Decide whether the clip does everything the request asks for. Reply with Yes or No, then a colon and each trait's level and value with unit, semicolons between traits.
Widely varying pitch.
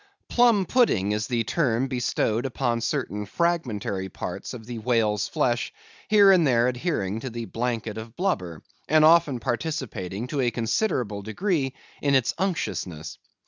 Yes: wide, 6.1 semitones